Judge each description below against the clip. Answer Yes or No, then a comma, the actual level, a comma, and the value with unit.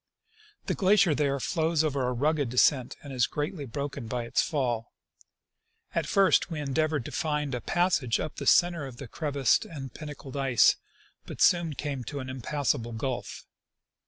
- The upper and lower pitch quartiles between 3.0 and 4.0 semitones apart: Yes, average, 3.4 semitones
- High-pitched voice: No, medium, 140 Hz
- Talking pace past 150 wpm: Yes, average, 165 wpm